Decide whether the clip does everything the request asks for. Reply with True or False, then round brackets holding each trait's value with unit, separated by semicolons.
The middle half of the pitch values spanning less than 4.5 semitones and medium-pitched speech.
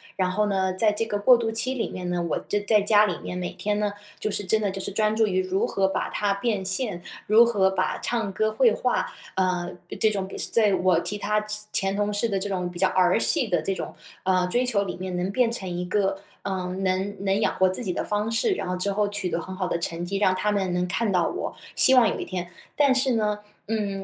False (2.5 semitones; 200 Hz)